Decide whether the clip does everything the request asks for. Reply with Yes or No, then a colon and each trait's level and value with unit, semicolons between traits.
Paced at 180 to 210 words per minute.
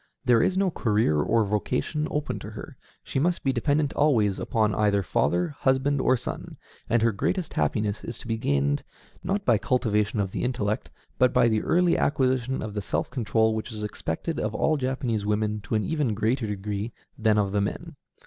Yes: average, 195 wpm